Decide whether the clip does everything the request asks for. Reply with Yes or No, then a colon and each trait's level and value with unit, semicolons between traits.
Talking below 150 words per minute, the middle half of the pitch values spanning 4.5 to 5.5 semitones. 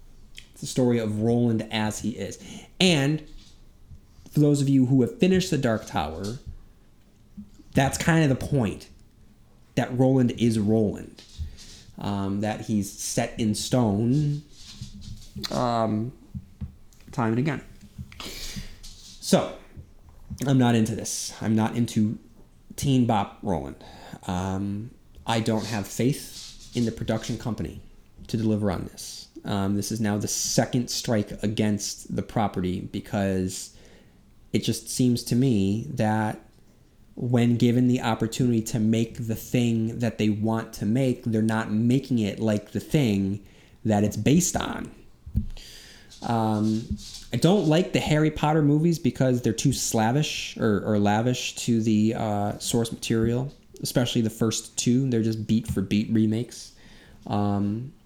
No: average, 140 wpm; average, 3.0 semitones